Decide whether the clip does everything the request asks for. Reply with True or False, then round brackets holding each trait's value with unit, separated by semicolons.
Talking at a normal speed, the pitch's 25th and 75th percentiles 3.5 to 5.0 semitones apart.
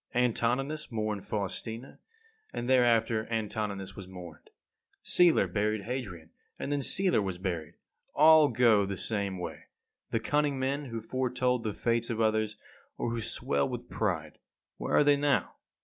True (150 wpm; 4.3 semitones)